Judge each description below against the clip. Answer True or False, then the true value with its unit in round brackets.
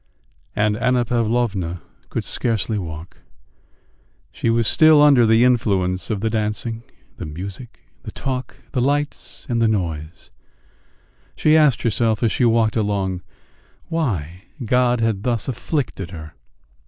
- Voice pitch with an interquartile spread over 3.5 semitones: True (4.2 semitones)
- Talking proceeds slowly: True (130 wpm)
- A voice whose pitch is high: False (115 Hz)